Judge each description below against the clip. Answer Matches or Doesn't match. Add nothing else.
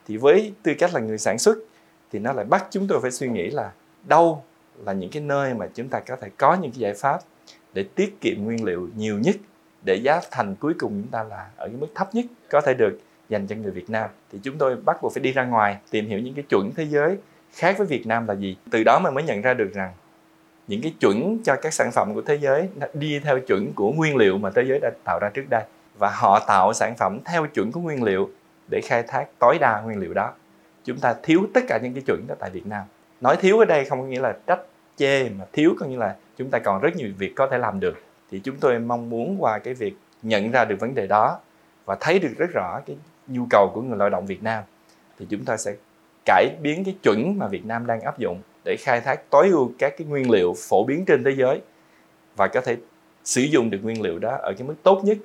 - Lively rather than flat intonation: Matches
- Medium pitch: Matches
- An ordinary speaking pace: Doesn't match